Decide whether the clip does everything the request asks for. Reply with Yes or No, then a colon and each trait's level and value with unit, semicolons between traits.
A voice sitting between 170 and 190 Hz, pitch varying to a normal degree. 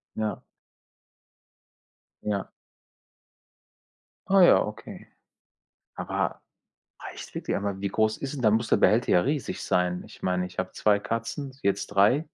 No: low, 105 Hz; average, 3.9 semitones